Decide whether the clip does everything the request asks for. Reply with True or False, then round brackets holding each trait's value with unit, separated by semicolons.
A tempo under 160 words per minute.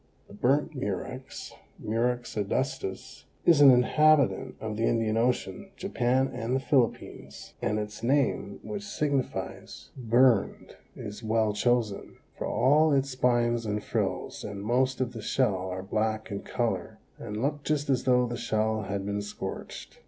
True (150 wpm)